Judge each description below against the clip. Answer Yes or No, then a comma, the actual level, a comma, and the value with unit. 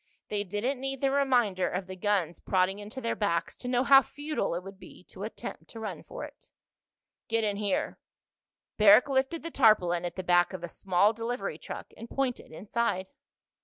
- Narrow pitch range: No, average, 5.0 semitones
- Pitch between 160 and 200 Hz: No, high, 210 Hz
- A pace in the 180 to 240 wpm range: Yes, average, 190 wpm